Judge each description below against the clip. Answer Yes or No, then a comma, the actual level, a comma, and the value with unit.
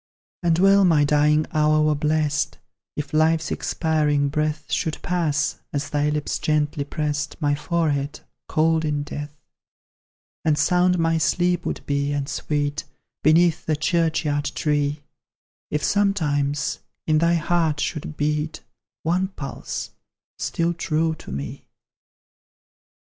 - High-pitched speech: No, medium, 155 Hz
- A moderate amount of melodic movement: No, narrow, 1.9 semitones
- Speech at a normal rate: No, slow, 125 wpm